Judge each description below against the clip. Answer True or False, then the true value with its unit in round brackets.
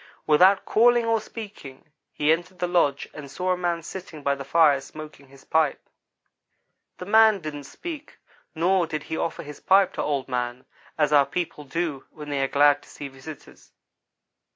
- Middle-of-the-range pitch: True (155 Hz)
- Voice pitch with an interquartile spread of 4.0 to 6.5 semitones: True (4.3 semitones)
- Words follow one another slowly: False (175 wpm)